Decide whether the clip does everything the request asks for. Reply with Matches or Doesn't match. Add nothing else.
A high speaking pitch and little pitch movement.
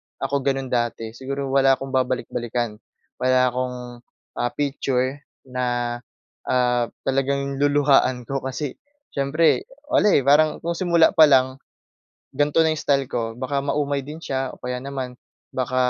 Doesn't match